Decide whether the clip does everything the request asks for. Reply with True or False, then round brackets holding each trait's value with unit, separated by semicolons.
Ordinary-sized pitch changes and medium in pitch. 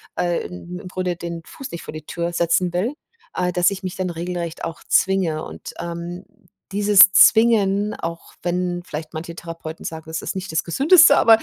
False (2.3 semitones; 175 Hz)